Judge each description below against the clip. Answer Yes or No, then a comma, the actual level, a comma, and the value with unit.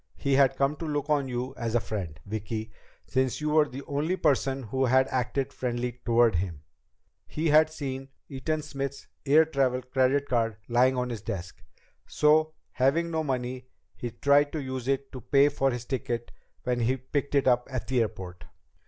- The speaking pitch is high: No, low, 130 Hz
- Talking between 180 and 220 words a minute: Yes, average, 185 wpm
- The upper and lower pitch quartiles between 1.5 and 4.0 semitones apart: Yes, average, 2.8 semitones